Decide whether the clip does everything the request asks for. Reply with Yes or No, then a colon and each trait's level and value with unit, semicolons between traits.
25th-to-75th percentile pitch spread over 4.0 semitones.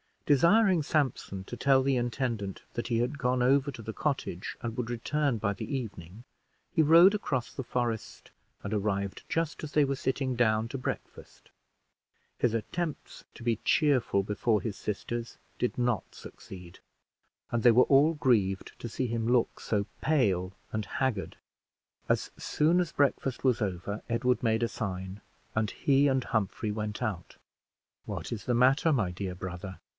Yes: average, 4.5 semitones